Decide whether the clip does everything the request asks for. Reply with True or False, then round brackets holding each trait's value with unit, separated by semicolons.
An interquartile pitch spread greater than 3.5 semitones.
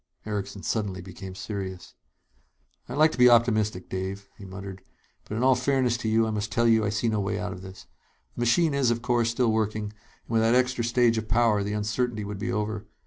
False (2.7 semitones)